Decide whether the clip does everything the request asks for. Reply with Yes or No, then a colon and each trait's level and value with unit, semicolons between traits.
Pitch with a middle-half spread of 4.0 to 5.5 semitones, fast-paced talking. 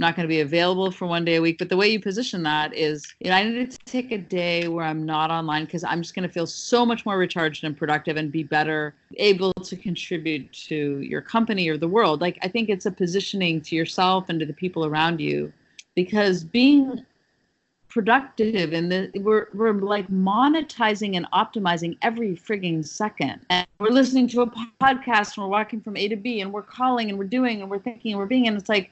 Yes: average, 4.8 semitones; fast, 225 wpm